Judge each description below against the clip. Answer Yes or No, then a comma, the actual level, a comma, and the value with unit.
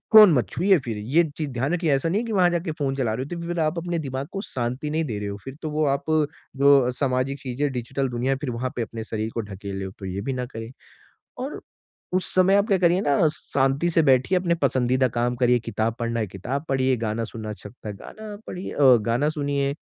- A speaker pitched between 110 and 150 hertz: Yes, low, 135 Hz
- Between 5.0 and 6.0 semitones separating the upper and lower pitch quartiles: Yes, wide, 5.4 semitones